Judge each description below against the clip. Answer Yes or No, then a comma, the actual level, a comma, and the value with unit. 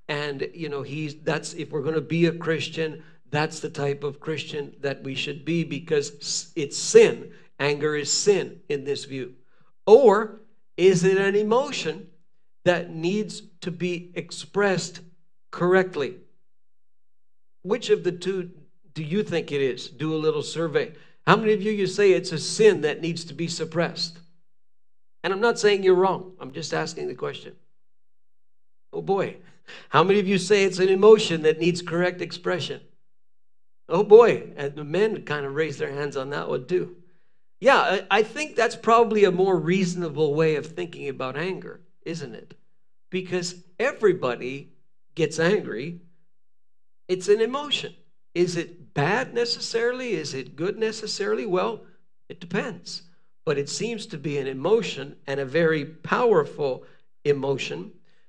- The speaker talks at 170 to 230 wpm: No, average, 155 wpm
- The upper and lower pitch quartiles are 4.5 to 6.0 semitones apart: Yes, average, 4.8 semitones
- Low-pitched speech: No, medium, 175 Hz